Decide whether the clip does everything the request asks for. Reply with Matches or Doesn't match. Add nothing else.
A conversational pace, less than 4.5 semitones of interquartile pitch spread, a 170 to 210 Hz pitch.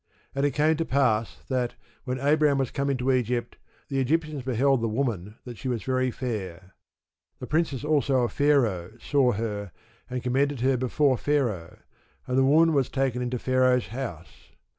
Doesn't match